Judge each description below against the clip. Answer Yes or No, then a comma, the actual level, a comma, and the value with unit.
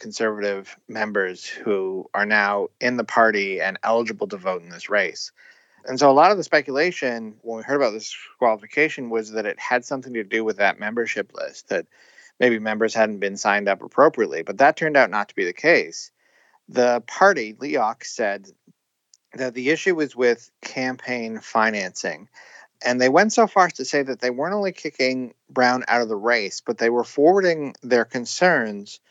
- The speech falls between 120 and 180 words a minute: No, average, 190 wpm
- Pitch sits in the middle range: No, low, 120 Hz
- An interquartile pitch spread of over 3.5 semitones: No, average, 3.2 semitones